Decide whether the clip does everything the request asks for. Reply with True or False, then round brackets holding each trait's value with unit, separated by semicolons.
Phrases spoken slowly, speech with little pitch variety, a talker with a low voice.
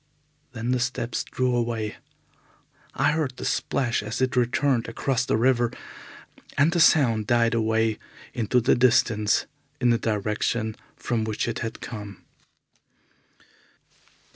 True (130 wpm; 2.3 semitones; 120 Hz)